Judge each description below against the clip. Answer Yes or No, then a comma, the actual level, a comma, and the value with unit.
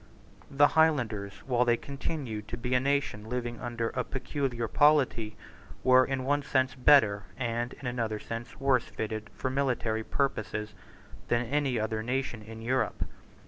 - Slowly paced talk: No, average, 150 wpm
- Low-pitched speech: Yes, low, 125 Hz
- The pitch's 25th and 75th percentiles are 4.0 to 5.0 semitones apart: No, average, 3.4 semitones